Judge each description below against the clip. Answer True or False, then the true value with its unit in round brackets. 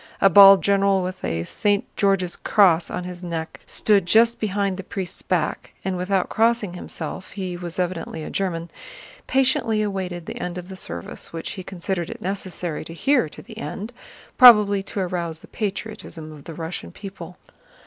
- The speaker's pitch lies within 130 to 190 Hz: True (185 Hz)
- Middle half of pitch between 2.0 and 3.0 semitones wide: True (2.7 semitones)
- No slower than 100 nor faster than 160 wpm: False (175 wpm)